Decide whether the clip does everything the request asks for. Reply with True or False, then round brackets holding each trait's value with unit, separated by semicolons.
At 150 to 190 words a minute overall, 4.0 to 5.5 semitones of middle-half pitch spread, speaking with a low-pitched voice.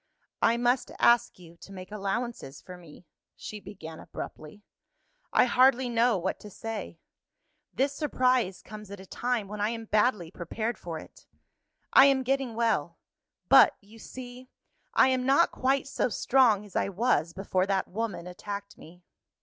False (160 wpm; 4.9 semitones; 215 Hz)